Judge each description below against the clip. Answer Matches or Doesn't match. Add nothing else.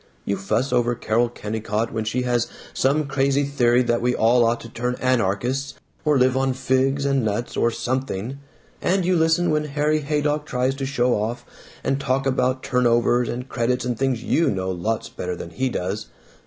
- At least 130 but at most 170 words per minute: Doesn't match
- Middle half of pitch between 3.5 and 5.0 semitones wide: Doesn't match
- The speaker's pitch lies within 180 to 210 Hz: Doesn't match